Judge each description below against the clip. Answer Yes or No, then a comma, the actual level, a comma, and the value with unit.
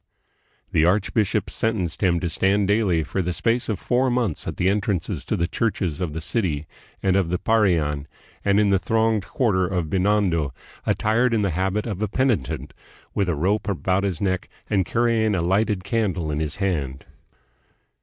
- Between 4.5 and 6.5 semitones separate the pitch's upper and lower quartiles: No, average, 3.8 semitones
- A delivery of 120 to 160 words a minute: No, average, 180 wpm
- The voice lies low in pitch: Yes, very low, 95 Hz